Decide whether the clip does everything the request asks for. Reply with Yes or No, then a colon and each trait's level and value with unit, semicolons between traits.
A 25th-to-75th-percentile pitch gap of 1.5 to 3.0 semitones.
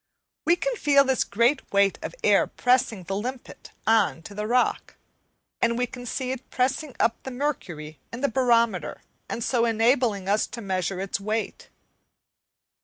No: average, 4.4 semitones